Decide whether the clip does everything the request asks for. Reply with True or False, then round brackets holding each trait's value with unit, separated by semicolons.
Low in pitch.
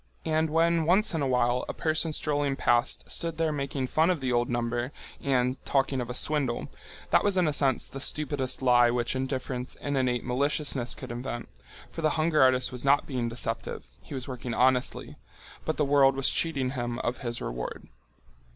True (130 Hz)